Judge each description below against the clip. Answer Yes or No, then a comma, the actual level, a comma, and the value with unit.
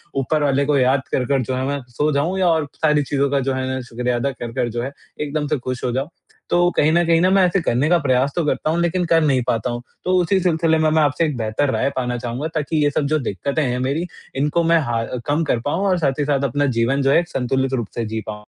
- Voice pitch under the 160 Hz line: Yes, medium, 140 Hz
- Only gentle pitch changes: No, average, 3.7 semitones